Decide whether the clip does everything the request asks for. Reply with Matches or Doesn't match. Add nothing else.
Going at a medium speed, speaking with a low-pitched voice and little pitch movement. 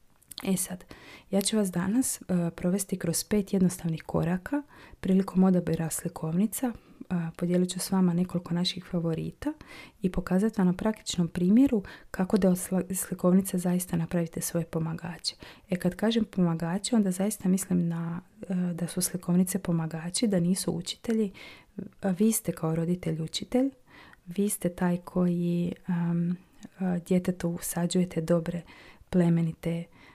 Doesn't match